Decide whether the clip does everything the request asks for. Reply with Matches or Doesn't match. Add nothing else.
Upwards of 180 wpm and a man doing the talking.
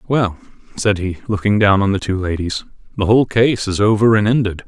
Matches